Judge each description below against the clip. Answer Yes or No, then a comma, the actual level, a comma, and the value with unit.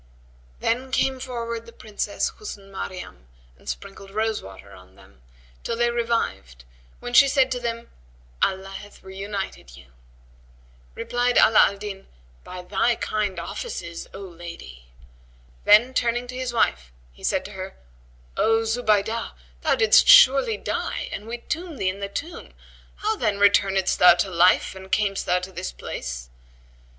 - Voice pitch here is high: Yes, high, 205 Hz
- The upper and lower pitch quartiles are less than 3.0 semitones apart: No, average, 4.5 semitones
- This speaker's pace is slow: No, average, 155 wpm